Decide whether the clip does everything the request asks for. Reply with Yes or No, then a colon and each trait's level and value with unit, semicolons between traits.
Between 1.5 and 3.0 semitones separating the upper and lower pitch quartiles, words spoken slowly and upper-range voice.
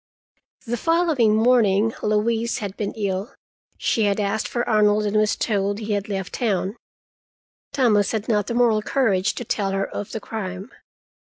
No: narrow, 2.4 semitones; average, 165 wpm; high, 215 Hz